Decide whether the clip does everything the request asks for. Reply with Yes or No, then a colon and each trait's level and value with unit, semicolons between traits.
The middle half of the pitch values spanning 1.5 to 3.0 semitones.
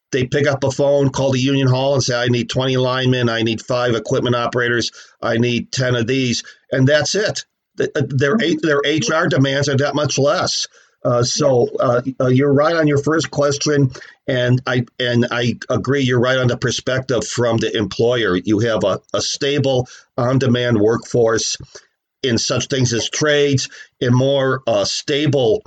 Yes: narrow, 2.5 semitones